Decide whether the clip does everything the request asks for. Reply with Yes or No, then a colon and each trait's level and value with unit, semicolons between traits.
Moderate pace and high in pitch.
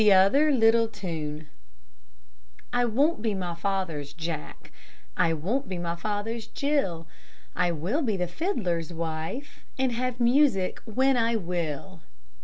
No: slow, 130 wpm; high, 200 Hz